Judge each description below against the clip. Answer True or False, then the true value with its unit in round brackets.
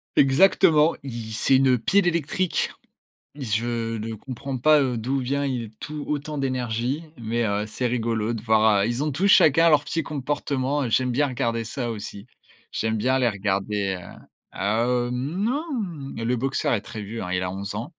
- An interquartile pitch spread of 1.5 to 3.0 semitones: False (4.2 semitones)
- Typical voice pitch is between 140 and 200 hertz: False (125 Hz)